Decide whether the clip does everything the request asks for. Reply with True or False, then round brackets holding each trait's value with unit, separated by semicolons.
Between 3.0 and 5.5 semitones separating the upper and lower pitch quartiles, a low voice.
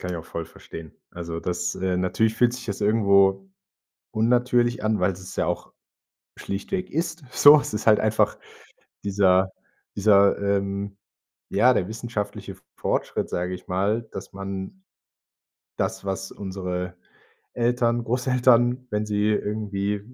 True (3.6 semitones; 100 Hz)